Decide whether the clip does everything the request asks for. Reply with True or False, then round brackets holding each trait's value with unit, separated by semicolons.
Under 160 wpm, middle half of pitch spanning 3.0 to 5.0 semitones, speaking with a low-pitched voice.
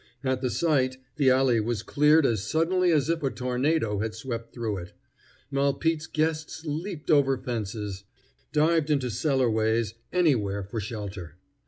False (145 wpm; 5.6 semitones; 130 Hz)